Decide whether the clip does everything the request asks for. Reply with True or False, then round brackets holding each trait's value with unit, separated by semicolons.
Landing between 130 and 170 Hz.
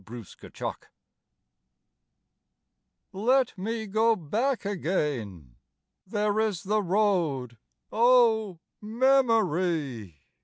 False (200 Hz)